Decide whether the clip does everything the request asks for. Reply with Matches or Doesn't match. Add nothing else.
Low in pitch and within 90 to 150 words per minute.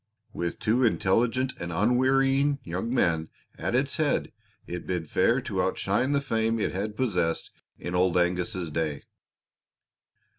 Matches